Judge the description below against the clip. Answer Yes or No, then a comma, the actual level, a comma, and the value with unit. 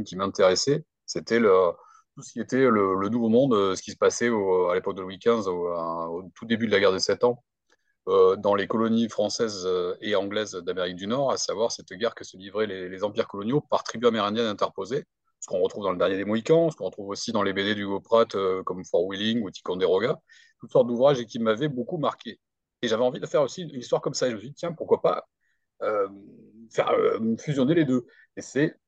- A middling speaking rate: No, fast, 235 wpm